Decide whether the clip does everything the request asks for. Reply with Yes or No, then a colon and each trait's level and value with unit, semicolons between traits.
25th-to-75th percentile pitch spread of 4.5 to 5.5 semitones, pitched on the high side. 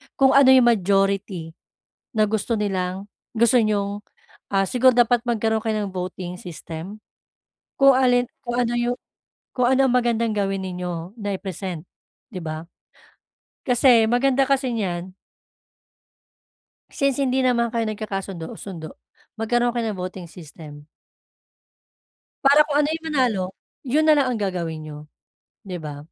Yes: average, 5.0 semitones; high, 215 Hz